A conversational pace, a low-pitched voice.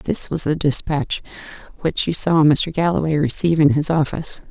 No: average, 175 wpm; medium, 155 Hz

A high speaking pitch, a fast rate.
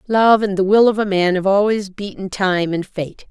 Yes: high, 195 Hz; fast, 235 wpm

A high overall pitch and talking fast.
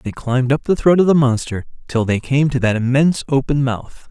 No: low, 130 Hz; fast, 235 wpm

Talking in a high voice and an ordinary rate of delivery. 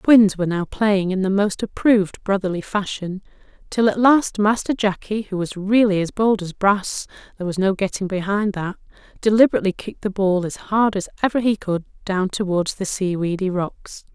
Yes: high, 200 Hz; average, 185 wpm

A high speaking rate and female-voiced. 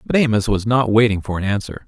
No: fast, 255 wpm; male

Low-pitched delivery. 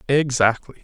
Yes: low, 130 Hz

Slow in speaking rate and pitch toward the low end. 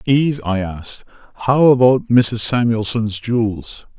Yes: slow, 120 wpm; low, 120 Hz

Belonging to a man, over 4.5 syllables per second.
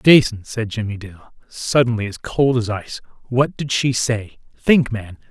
No: male; 4.4 syllables/s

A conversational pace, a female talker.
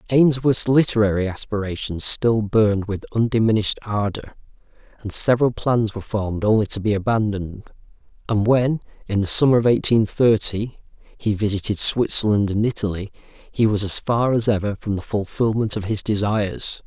No: average, 150 wpm; male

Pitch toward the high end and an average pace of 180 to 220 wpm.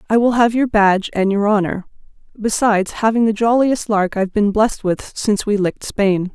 Yes: high, 210 Hz; average, 200 wpm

